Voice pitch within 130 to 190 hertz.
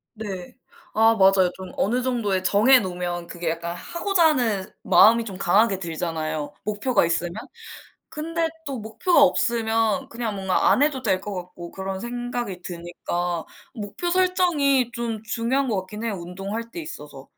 No: high, 210 Hz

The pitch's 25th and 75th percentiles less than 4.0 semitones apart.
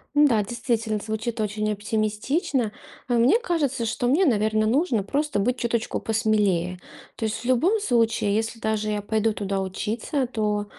Yes: average, 2.8 semitones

